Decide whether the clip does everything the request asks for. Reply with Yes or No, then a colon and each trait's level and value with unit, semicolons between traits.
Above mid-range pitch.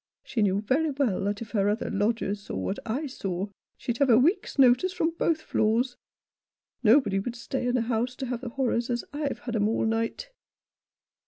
Yes: high, 240 Hz